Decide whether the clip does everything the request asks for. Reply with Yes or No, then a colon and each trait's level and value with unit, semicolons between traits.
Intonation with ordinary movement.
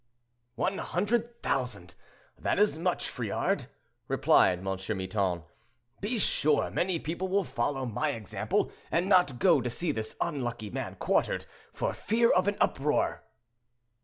No: wide, 8.8 semitones